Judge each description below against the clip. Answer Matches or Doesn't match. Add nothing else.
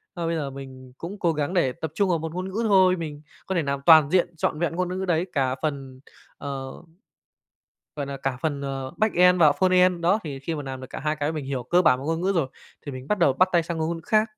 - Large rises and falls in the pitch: Doesn't match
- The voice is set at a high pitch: Doesn't match